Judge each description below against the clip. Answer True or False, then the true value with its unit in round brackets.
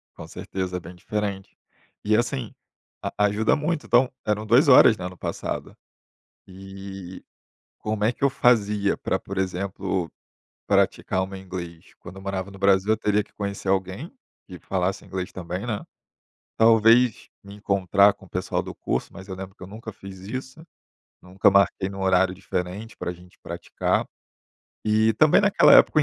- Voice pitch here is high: False (100 Hz)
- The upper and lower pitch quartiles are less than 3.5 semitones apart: True (2.4 semitones)